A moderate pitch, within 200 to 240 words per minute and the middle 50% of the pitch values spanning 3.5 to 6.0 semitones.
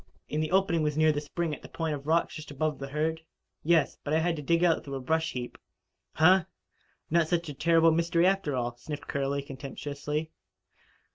No: medium, 155 Hz; fast, 205 wpm; average, 2.7 semitones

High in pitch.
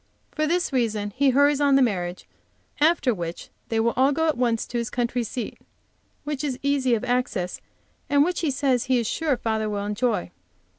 Yes: very high, 250 Hz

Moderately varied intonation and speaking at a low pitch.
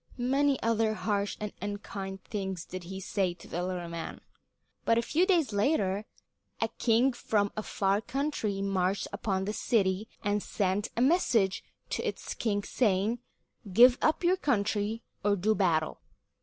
No: average, 3.3 semitones; high, 205 Hz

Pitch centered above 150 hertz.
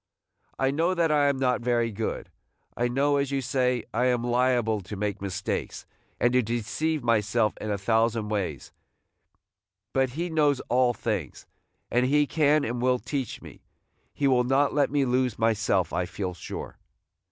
No: low, 125 Hz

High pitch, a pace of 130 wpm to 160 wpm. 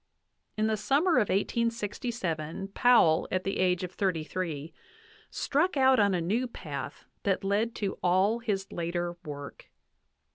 Yes: high, 195 Hz; average, 145 wpm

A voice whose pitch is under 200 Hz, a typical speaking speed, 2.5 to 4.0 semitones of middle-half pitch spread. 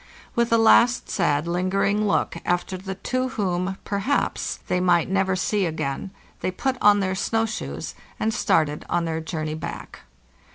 Yes: high, 190 Hz; average, 160 wpm; average, 3.5 semitones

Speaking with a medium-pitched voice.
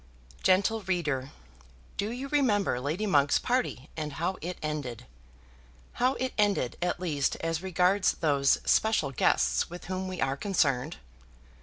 Yes: medium, 175 Hz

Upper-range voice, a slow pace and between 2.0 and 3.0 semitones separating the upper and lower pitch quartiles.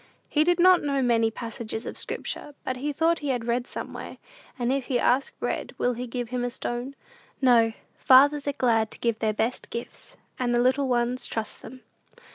No: high, 245 Hz; average, 195 wpm; average, 2.7 semitones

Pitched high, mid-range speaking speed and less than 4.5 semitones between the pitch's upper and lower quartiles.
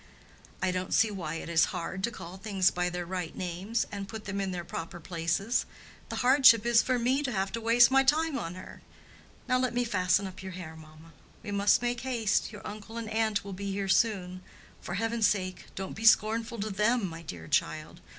No: high, 200 Hz; fast, 215 wpm; average, 4.1 semitones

